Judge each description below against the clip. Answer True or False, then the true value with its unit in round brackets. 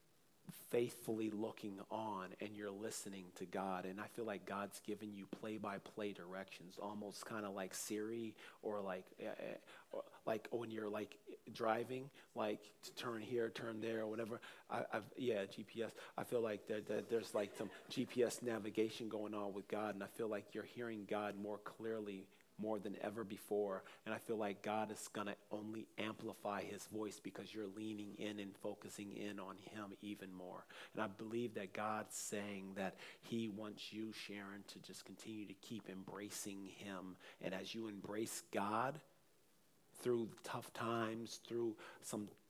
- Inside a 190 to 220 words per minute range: False (170 wpm)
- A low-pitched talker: True (105 Hz)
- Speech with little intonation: True (1.7 semitones)